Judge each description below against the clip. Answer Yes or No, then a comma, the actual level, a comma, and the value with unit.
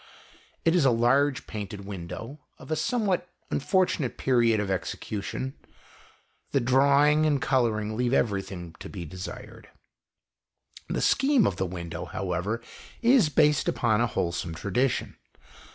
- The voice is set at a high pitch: No, low, 120 Hz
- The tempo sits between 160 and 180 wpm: No, slow, 135 wpm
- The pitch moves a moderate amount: No, wide, 6.8 semitones